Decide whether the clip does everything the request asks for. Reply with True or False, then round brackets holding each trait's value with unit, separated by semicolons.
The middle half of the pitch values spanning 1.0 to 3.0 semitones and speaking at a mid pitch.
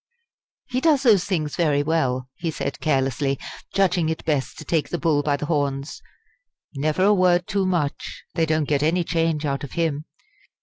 False (3.4 semitones; 155 Hz)